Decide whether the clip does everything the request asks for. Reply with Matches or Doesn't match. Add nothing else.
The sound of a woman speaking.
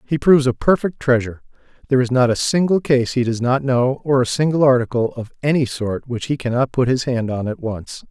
Doesn't match